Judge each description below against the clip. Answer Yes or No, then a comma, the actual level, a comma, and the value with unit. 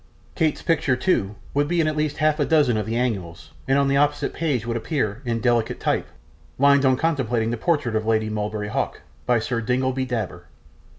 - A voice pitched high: No, low, 125 Hz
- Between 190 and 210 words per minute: Yes, average, 200 wpm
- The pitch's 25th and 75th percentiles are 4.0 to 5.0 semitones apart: Yes, average, 4.7 semitones